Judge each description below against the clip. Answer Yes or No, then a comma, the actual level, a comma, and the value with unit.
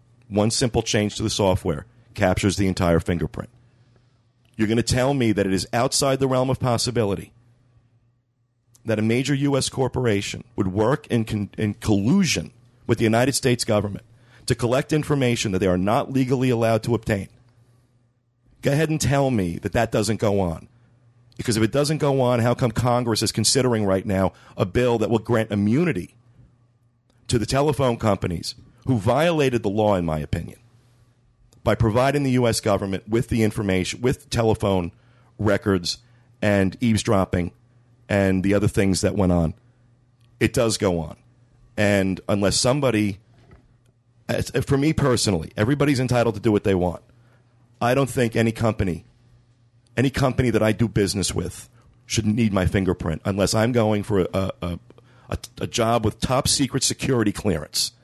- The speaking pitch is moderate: No, low, 115 Hz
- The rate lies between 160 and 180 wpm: Yes, average, 165 wpm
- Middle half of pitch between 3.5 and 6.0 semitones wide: No, average, 3.0 semitones